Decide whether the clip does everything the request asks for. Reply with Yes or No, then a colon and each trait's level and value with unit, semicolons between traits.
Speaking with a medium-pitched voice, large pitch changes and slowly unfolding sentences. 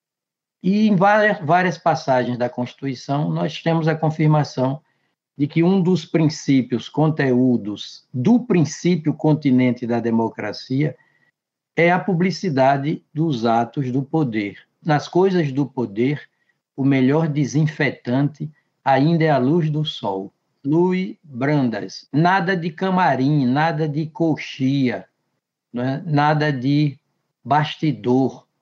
No: medium, 150 Hz; average, 4.0 semitones; slow, 115 wpm